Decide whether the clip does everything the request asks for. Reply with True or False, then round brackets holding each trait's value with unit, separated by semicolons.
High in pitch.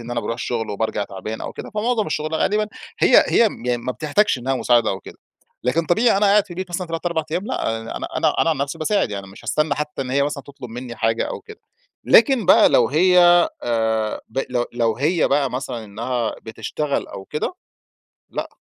False (135 Hz)